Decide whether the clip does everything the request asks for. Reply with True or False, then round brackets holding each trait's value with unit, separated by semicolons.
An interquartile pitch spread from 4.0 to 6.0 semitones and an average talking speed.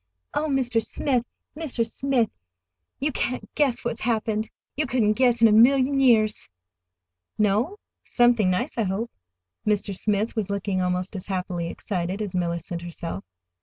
True (4.5 semitones; 145 wpm)